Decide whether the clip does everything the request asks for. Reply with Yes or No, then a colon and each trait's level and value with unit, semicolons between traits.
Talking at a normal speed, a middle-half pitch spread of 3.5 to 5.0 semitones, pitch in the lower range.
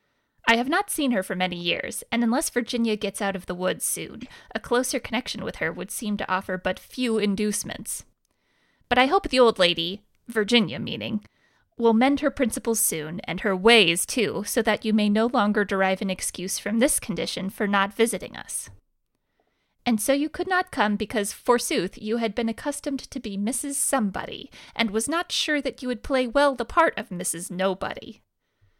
No: average, 190 wpm; average, 4.6 semitones; high, 220 Hz